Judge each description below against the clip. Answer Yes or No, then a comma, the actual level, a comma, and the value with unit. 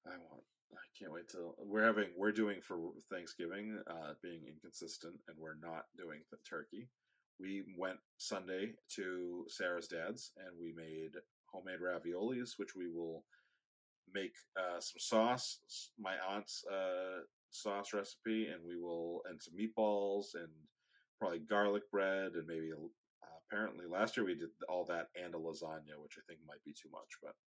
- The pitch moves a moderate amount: Yes, average, 3.6 semitones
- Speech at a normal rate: Yes, average, 165 wpm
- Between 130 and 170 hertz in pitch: No, very low, 95 Hz